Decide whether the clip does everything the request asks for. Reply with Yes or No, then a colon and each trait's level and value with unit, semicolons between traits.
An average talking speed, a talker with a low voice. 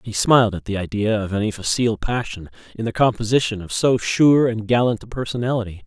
Yes: average, 195 wpm; low, 110 Hz